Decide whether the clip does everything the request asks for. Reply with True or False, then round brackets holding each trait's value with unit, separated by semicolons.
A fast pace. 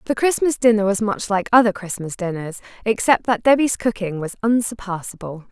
False (165 wpm)